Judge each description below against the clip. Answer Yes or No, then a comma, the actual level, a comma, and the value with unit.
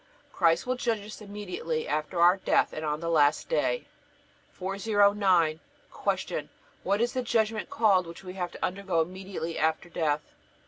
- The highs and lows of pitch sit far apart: No, average, 3.9 semitones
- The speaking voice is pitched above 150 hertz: Yes, medium, 185 Hz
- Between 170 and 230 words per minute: No, average, 155 wpm